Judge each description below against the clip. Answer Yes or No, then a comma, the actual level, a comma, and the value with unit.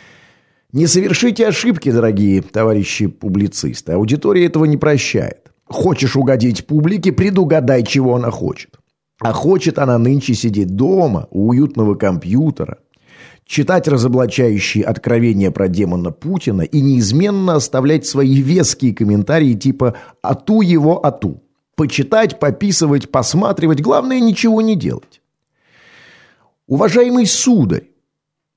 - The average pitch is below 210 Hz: Yes, medium, 140 Hz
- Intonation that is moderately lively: No, wide, 7.0 semitones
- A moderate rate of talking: No, slow, 105 wpm